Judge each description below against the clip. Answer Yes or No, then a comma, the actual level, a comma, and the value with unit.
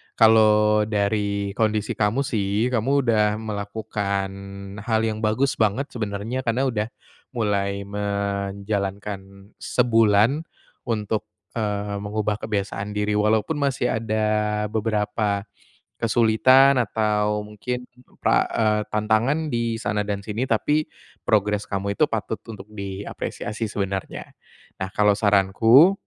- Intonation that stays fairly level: Yes, narrow, 1.8 semitones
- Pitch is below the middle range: Yes, low, 105 Hz